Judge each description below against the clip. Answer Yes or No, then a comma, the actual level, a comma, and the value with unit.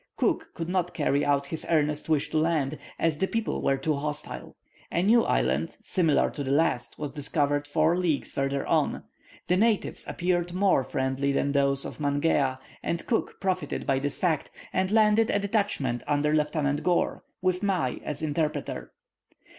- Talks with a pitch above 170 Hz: No, medium, 155 Hz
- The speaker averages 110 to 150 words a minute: No, average, 170 wpm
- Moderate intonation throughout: Yes, average, 4.1 semitones